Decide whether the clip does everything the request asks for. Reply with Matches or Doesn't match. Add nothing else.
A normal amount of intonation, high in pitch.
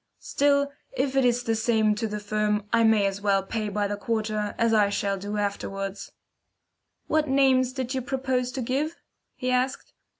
Matches